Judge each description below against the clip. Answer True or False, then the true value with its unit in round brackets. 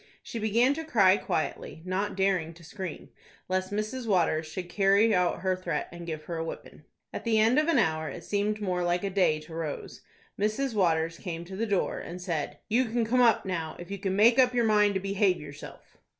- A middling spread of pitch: True (4.1 semitones)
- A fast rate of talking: True (210 wpm)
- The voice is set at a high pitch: True (195 Hz)